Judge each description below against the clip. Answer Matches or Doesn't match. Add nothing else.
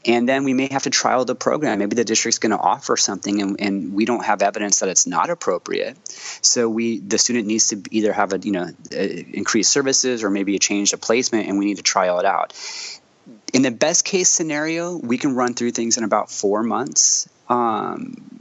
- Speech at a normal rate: Doesn't match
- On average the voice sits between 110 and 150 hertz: Matches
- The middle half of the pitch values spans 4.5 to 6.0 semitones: Matches